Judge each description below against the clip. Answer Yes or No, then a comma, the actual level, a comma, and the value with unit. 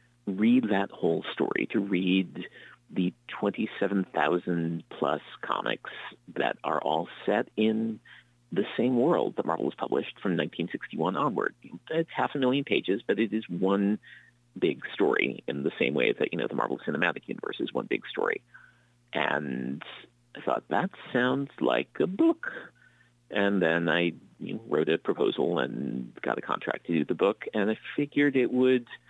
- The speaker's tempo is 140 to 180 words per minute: Yes, average, 165 wpm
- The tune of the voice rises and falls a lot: Yes, wide, 5.9 semitones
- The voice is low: Yes, low, 110 Hz